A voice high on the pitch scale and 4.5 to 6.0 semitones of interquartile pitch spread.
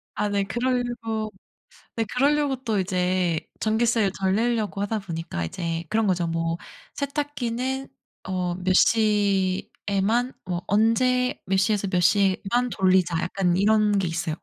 No: high, 205 Hz; average, 4.0 semitones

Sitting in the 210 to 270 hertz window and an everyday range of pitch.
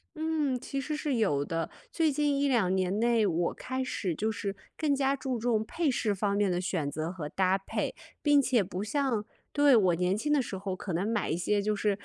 No: high, 215 Hz; wide, 6.4 semitones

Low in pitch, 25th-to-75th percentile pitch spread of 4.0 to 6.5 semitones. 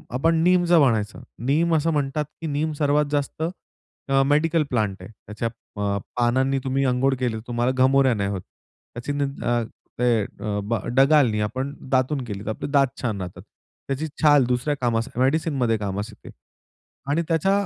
Yes: low, 130 Hz; average, 4.4 semitones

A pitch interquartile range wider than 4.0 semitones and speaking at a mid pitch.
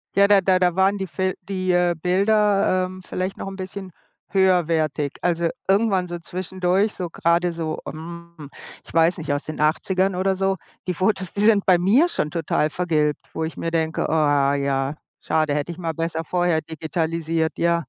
No: average, 2.8 semitones; medium, 175 Hz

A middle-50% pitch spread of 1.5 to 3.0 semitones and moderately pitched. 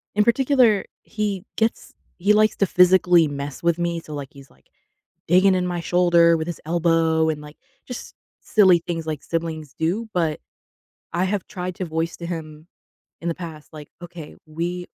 Yes: narrow, 2.4 semitones; medium, 170 Hz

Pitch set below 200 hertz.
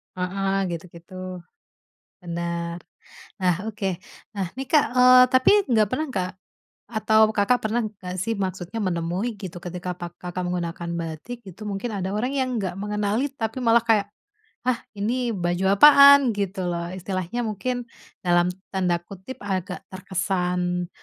Yes: high, 190 Hz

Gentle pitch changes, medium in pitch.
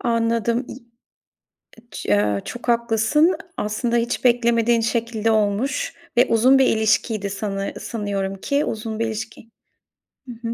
No: narrow, 2.1 semitones; high, 230 Hz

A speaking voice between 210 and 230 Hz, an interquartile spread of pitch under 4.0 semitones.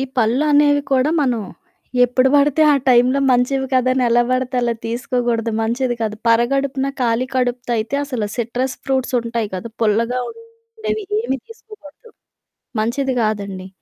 No: very high, 255 Hz; average, 2.9 semitones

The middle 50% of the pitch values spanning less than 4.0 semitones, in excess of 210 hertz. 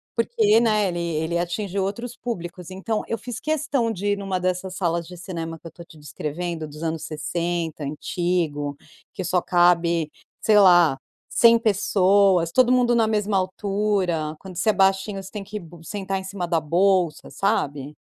No: average, 3.5 semitones; medium, 185 Hz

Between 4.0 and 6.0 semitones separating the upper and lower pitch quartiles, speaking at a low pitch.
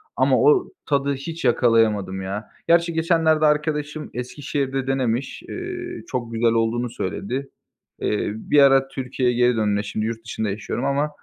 Yes: average, 4.9 semitones; low, 130 Hz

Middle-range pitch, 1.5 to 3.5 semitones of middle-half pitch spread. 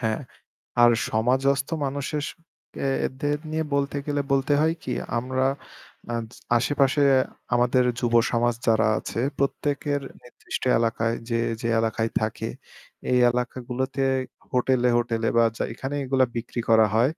No: low, 125 Hz; average, 2.9 semitones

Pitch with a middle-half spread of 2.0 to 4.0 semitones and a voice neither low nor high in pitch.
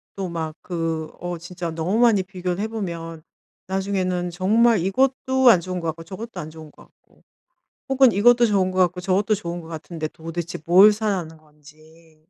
Yes: average, 3.6 semitones; medium, 180 Hz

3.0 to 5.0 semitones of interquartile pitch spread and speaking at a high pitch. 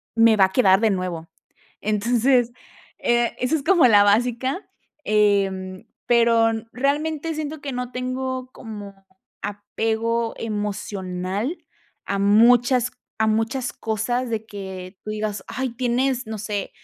Yes: average, 3.6 semitones; high, 225 Hz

